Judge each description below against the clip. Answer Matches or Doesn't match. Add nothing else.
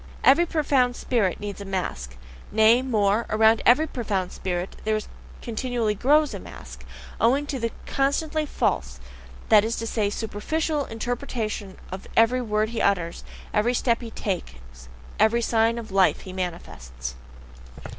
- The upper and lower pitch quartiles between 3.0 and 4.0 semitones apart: Doesn't match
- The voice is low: Doesn't match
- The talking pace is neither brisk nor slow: Matches